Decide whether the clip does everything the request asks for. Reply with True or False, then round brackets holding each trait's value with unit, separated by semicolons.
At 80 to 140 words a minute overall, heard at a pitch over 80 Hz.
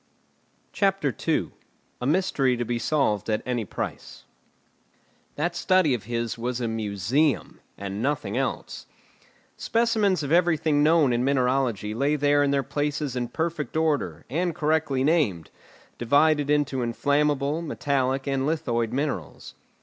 True (135 wpm; 140 Hz)